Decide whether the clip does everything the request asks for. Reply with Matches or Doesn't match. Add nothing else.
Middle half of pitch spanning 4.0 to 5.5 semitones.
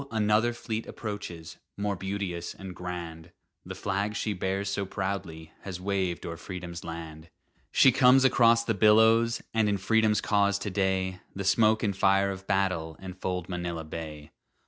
Doesn't match